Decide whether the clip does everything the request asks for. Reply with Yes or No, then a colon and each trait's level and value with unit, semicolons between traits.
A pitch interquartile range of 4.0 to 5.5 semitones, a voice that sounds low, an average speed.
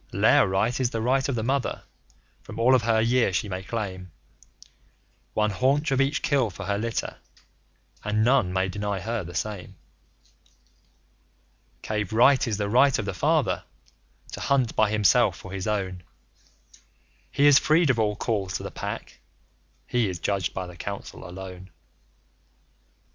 Yes: average, 4.5 semitones; low, 105 Hz; average, 160 wpm